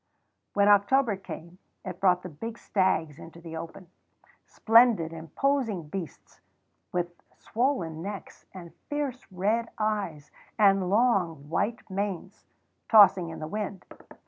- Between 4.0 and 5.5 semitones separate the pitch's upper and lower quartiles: Yes, average, 4.3 semitones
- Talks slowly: Yes, slow, 120 wpm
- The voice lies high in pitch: Yes, high, 195 Hz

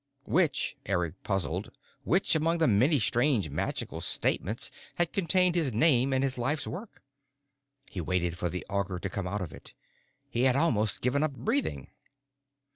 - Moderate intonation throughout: No, wide, 8.3 semitones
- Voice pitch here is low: Yes, low, 120 Hz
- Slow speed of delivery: No, average, 160 wpm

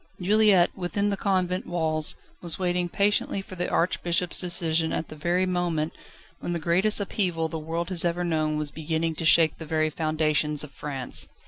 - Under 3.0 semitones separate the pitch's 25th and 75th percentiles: Yes, narrow, 2.5 semitones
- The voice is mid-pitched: Yes, medium, 170 Hz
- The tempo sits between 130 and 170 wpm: No, average, 180 wpm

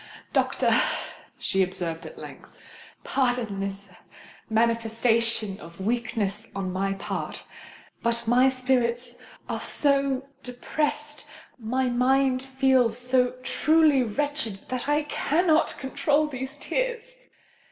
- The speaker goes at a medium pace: No, slow, 100 wpm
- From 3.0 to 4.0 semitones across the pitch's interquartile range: Yes, average, 3.6 semitones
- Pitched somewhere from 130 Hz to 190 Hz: No, very high, 250 Hz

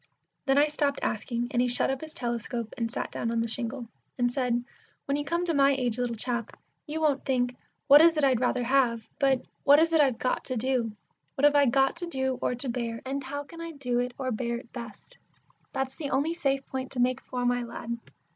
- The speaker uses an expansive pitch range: No, average, 2.7 semitones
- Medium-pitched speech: No, very high, 260 Hz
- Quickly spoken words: Yes, fast, 235 wpm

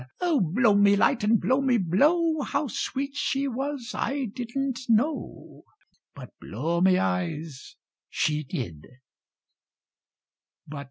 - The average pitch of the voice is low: No, high, 235 Hz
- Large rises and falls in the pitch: Yes, wide, 7.8 semitones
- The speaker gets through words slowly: Yes, slow, 115 wpm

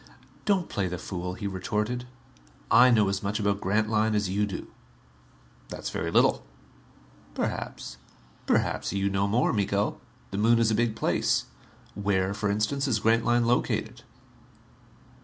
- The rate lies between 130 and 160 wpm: Yes, average, 140 wpm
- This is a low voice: Yes, low, 105 Hz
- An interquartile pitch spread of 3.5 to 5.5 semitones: No, narrow, 2.5 semitones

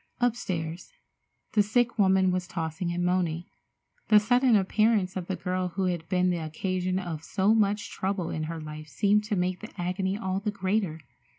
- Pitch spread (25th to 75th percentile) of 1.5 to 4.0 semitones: Yes, average, 2.9 semitones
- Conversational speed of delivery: Yes, average, 180 wpm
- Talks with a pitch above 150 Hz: Yes, medium, 185 Hz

